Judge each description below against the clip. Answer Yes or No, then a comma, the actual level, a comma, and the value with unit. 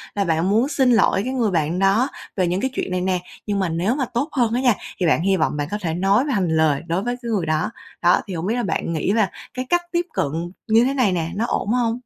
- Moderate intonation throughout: No, wide, 5.8 semitones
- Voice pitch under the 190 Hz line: No, high, 195 Hz